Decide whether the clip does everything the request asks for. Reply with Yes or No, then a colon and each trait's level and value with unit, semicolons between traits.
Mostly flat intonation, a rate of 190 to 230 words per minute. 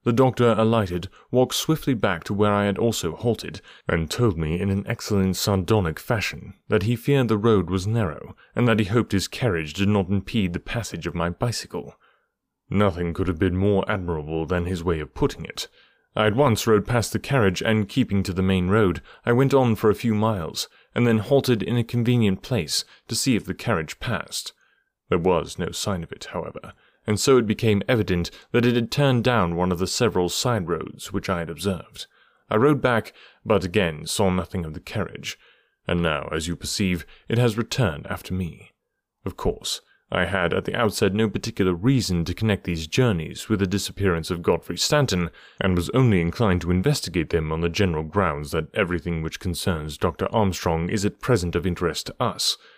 No: average, 4.5 semitones; average, 200 wpm